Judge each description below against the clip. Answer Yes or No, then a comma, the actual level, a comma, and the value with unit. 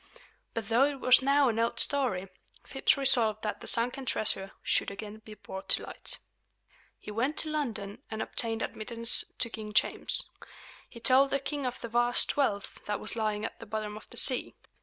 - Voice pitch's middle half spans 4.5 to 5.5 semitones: No, average, 3.4 semitones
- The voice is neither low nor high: No, high, 230 Hz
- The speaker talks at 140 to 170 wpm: No, average, 190 wpm